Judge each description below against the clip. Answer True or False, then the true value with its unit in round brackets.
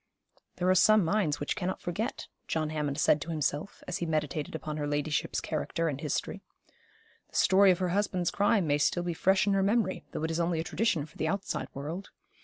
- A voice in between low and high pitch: True (170 Hz)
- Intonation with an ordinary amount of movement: True (3.9 semitones)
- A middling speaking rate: False (210 wpm)